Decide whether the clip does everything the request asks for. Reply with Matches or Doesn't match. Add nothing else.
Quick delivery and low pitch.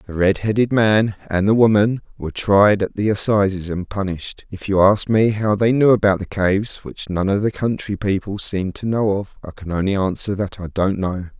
Matches